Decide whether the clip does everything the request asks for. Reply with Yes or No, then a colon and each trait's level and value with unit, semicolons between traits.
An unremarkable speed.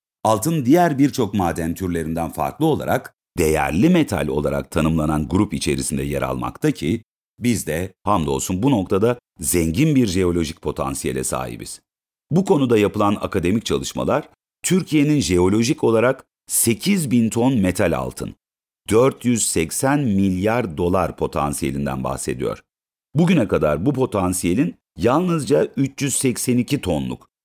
Yes: average, 110 wpm